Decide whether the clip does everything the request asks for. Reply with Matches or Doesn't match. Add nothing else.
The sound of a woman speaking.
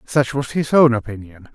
Doesn't match